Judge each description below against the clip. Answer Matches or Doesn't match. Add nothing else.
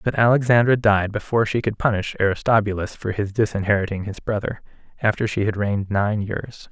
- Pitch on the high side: Doesn't match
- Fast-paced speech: Doesn't match